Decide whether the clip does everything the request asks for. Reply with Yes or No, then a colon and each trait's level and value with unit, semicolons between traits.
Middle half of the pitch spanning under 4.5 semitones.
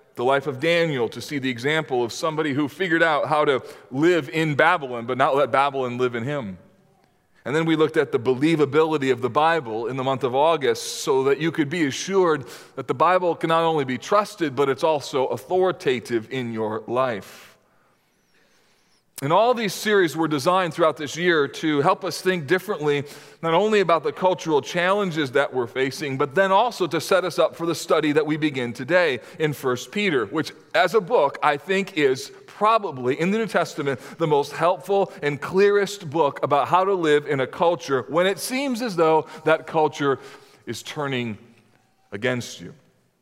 No: average, 4.9 semitones